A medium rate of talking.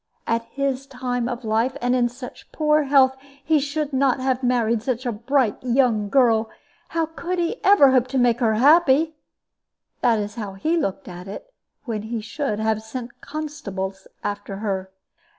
Yes: average, 170 wpm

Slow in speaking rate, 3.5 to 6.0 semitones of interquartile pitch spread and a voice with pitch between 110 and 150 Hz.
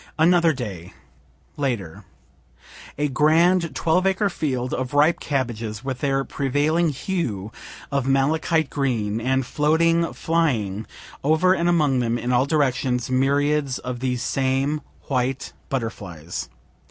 Yes: slow, 120 wpm; average, 4.2 semitones; low, 135 Hz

